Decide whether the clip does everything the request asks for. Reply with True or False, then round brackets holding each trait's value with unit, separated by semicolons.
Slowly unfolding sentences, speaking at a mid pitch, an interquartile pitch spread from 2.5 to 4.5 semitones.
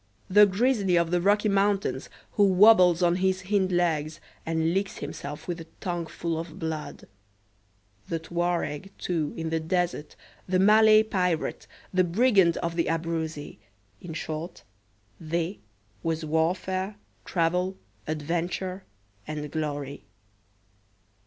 True (125 wpm; 175 Hz; 2.8 semitones)